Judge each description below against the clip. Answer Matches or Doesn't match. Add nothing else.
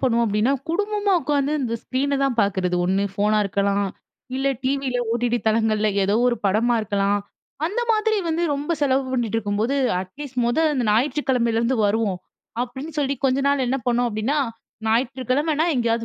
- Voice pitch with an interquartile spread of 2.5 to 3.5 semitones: Doesn't match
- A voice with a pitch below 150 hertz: Doesn't match